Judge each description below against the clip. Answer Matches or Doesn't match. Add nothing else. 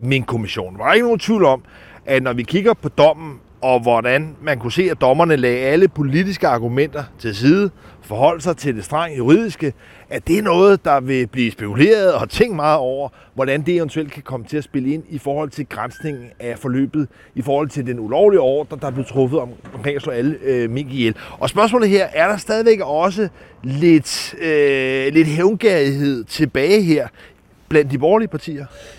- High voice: Doesn't match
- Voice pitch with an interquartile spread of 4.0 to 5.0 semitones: Matches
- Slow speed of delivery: Doesn't match